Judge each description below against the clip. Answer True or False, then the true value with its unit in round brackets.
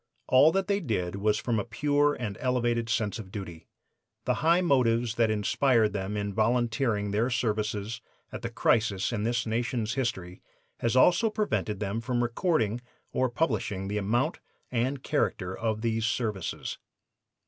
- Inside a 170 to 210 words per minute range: False (155 wpm)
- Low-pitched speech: True (115 Hz)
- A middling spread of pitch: True (3.3 semitones)